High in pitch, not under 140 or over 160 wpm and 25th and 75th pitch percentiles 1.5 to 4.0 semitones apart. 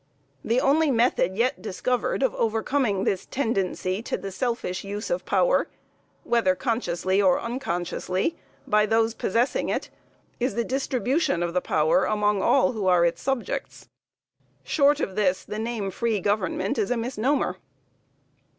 No: high, 225 Hz; average, 145 wpm; average, 5.0 semitones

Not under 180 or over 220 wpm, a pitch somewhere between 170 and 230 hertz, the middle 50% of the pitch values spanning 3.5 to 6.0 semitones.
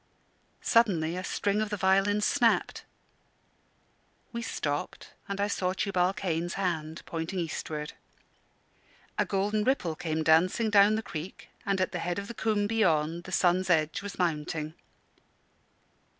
No: average, 140 wpm; medium, 185 Hz; average, 3.9 semitones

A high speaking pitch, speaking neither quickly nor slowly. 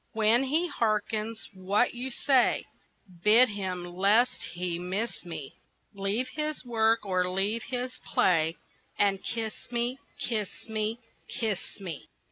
No: high, 215 Hz; slow, 125 wpm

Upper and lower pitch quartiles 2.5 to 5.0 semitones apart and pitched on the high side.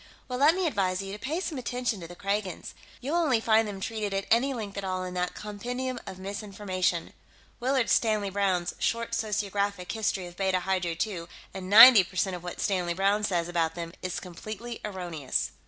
Yes: average, 3.7 semitones; high, 200 Hz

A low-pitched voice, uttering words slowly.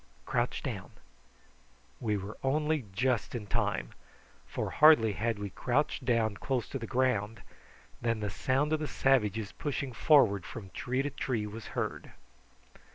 No: low, 120 Hz; average, 155 wpm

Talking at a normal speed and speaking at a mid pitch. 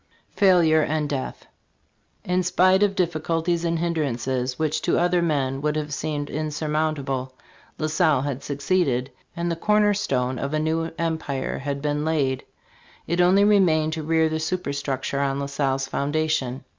Yes: average, 155 wpm; medium, 155 Hz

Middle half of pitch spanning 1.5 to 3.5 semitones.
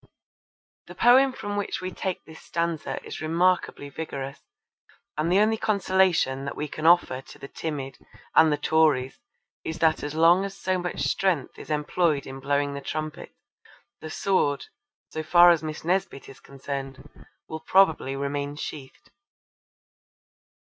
No: average, 4.2 semitones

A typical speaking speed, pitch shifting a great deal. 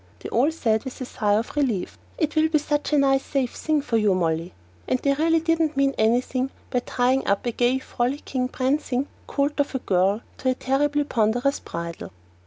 No: average, 195 wpm; average, 4.1 semitones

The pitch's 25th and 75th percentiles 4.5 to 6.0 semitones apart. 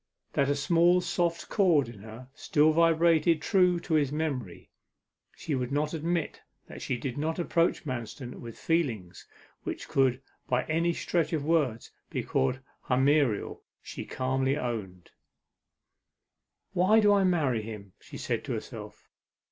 Yes: average, 5.1 semitones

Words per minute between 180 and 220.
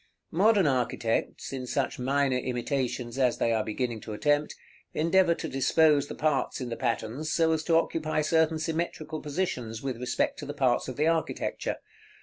No: average, 170 wpm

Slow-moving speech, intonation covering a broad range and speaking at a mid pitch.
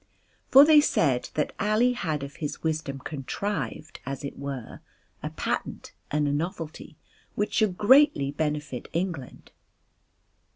Yes: slow, 130 wpm; wide, 6.7 semitones; medium, 155 Hz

